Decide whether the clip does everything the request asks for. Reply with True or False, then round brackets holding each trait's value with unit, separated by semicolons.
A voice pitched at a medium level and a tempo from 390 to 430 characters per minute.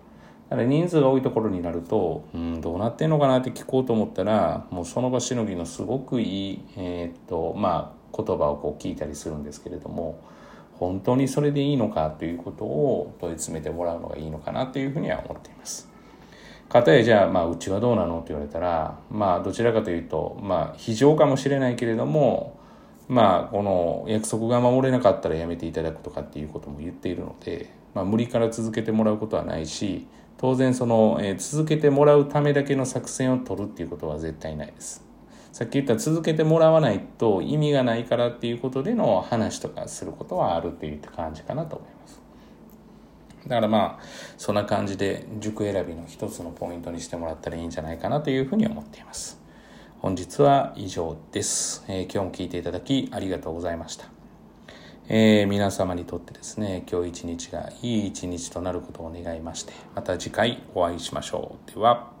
False (105 Hz; 415 characters per minute)